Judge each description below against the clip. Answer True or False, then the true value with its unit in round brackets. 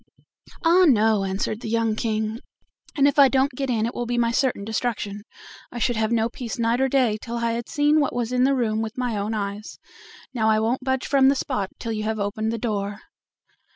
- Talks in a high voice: True (230 Hz)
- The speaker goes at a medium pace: False (220 wpm)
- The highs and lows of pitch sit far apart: False (2.8 semitones)